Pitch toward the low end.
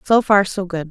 No: high, 190 Hz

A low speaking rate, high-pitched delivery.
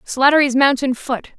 Yes: slow, 130 wpm; very high, 265 Hz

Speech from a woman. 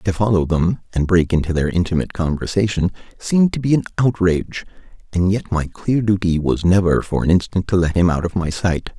No: male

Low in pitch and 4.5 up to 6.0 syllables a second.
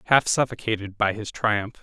Yes: low, 110 Hz; 5.1 syllables/s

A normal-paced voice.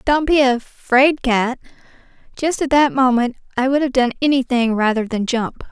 Yes: average, 170 wpm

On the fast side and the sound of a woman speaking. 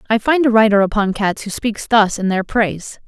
Yes: fast, 235 wpm; female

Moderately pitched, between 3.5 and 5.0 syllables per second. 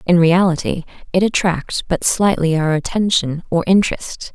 Yes: medium, 175 Hz; 4.7 syllables/s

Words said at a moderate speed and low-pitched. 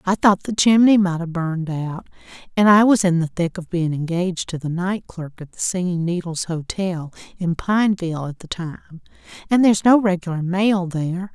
No: average, 185 wpm; medium, 180 Hz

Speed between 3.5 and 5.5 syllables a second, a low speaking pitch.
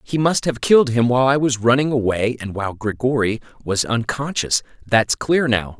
Yes: 5.2 syllables/s; low, 120 Hz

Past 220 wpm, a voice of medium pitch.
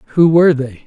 No: fast, 205 wpm; medium, 145 Hz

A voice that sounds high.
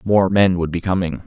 No: very low, 90 Hz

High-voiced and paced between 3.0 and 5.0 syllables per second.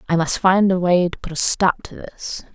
No: medium, 180 Hz; 4.8 syllables/s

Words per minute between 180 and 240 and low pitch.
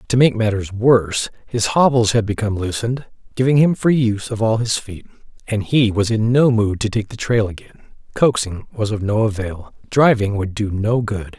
Yes: average, 200 wpm; low, 110 Hz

